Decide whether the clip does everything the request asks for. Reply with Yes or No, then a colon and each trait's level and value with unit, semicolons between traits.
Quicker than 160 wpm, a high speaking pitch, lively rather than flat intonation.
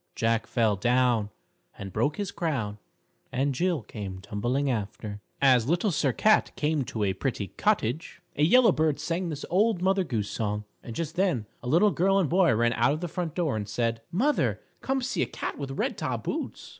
No: average, 195 wpm; medium, 140 Hz; wide, 7.7 semitones